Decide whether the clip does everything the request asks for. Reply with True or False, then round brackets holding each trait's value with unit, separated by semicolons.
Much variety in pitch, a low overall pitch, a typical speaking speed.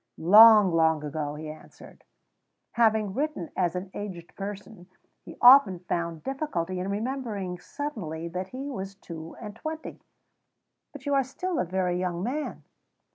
False (6.0 semitones; 190 Hz; 145 wpm)